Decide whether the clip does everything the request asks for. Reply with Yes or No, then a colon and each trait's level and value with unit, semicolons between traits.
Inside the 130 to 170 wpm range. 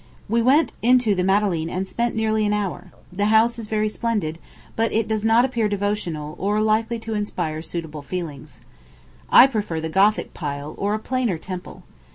No: average, 180 wpm